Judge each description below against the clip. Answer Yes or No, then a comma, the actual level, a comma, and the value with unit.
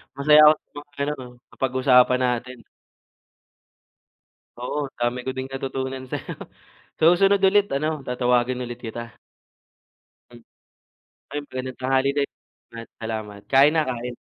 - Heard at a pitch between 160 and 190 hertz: No, low, 130 Hz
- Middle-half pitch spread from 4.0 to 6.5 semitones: No, narrow, 2.6 semitones